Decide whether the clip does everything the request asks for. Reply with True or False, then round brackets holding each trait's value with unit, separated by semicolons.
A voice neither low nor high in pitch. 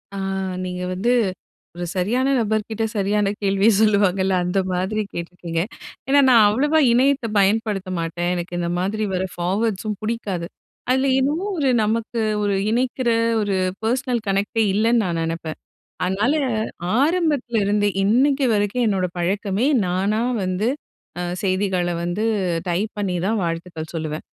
False (205 Hz)